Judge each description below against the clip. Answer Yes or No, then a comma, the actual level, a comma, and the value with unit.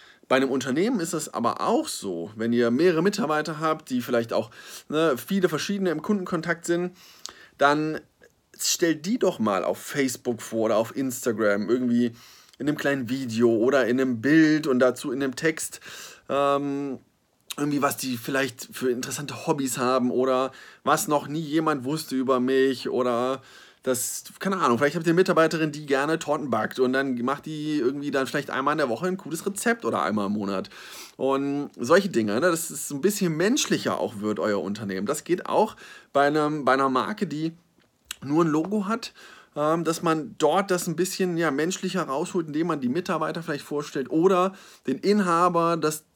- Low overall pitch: No, medium, 145 Hz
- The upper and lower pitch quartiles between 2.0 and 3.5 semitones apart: No, average, 4.4 semitones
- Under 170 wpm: No, average, 180 wpm